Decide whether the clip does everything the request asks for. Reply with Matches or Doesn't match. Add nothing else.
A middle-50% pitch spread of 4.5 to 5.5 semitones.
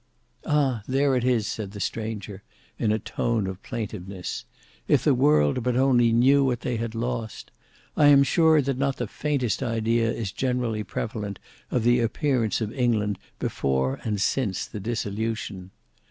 Doesn't match